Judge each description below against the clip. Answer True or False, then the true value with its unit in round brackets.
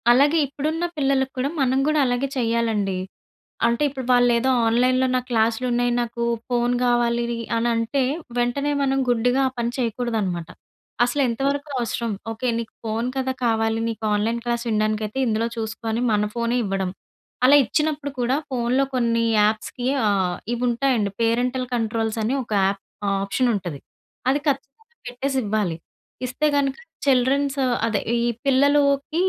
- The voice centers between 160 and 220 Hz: False (240 Hz)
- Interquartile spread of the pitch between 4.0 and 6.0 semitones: False (2.9 semitones)